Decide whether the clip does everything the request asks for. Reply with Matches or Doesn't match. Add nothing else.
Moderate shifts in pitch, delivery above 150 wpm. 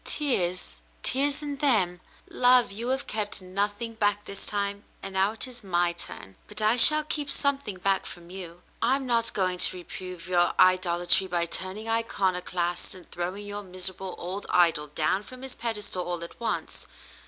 Matches